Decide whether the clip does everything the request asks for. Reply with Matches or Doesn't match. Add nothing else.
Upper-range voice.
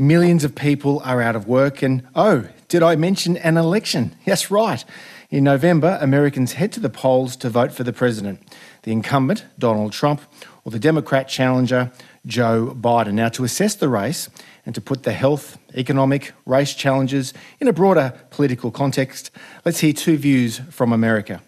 Doesn't match